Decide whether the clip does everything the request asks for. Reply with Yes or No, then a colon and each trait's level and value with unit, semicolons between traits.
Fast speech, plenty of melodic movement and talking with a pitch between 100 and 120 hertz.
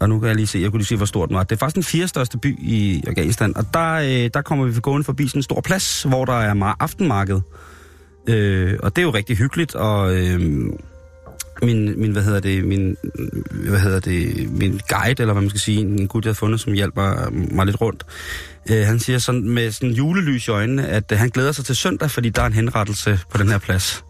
No: fast, 245 wpm; average, 4.2 semitones; low, 110 Hz